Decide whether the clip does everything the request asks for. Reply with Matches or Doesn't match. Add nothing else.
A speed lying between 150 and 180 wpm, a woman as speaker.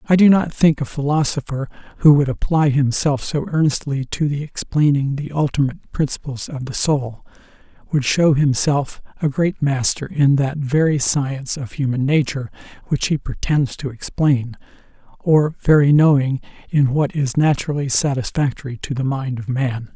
Doesn't match